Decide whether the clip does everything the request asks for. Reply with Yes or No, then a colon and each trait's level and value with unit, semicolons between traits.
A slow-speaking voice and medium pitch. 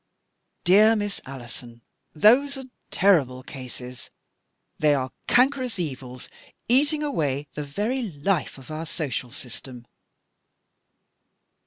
Yes: slow, 110 wpm; medium, 150 Hz